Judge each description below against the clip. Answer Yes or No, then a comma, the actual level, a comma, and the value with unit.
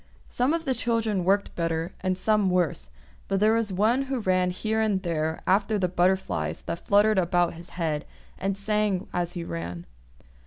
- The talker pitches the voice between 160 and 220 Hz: Yes, high, 190 Hz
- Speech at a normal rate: Yes, average, 180 wpm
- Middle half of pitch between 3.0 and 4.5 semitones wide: Yes, average, 3.6 semitones